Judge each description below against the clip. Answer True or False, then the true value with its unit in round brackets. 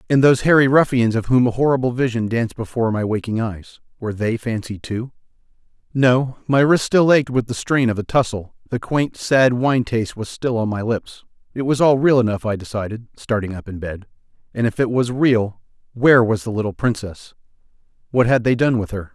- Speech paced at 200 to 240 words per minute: True (205 wpm)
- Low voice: True (120 Hz)